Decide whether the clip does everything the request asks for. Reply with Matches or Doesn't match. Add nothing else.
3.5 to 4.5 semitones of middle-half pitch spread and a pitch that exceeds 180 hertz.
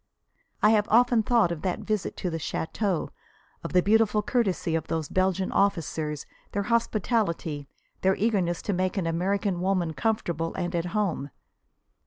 Matches